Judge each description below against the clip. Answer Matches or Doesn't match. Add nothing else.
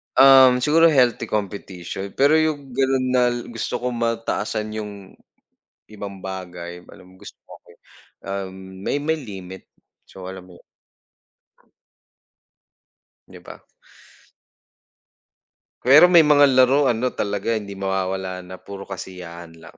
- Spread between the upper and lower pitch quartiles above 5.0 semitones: Matches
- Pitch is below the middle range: Matches